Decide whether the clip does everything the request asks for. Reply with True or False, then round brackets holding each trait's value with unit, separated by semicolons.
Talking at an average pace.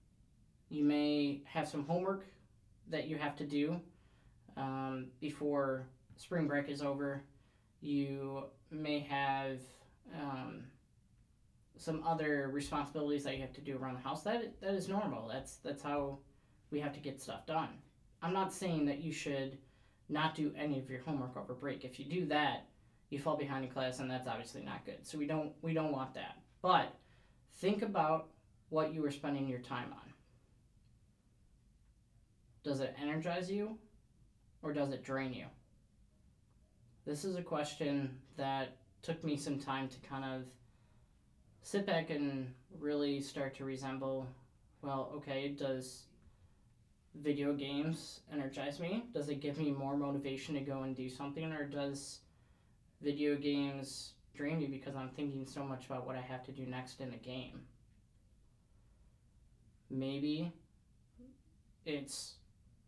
True (150 wpm)